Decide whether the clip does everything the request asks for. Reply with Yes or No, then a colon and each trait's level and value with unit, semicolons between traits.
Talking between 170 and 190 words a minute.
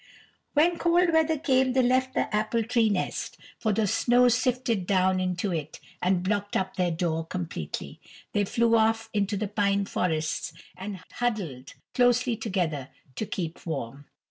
No: average, 155 wpm